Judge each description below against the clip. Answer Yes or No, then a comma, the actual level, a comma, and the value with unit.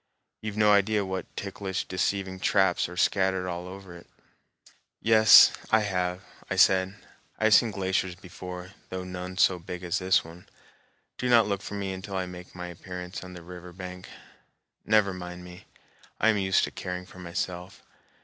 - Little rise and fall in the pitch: Yes, narrow, 1.6 semitones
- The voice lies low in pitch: Yes, very low, 95 Hz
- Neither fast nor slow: Yes, average, 170 wpm